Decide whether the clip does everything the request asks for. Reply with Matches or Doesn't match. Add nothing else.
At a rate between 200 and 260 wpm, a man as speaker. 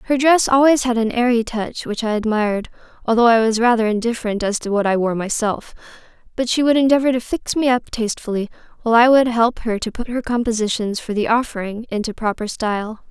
Doesn't match